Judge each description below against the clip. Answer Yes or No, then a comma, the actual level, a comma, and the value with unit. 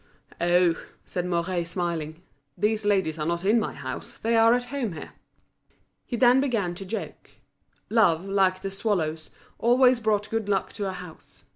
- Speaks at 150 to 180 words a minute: Yes, average, 165 wpm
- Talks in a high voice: Yes, high, 195 Hz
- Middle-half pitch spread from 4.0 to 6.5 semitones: Yes, average, 4.6 semitones